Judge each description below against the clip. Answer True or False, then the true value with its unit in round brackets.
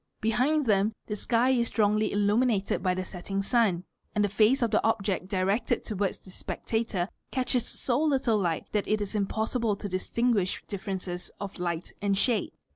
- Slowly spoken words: False (185 wpm)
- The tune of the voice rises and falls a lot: False (3.2 semitones)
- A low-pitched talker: False (210 Hz)